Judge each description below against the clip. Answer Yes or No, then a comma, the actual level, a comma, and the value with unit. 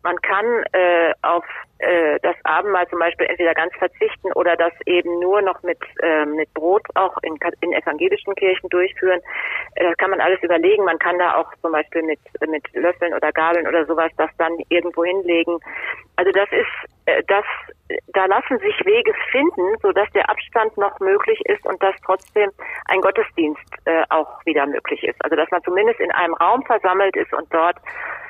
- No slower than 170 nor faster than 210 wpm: Yes, average, 185 wpm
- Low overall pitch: No, medium, 185 Hz